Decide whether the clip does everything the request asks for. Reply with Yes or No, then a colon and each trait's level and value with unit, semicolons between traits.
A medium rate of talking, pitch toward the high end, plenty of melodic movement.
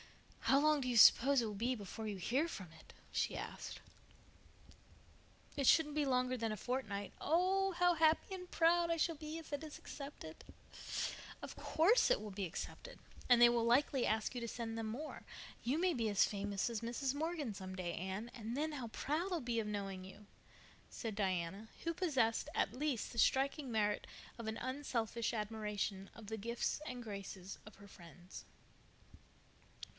Yes: average, 180 wpm; high, 235 Hz; wide, 6.0 semitones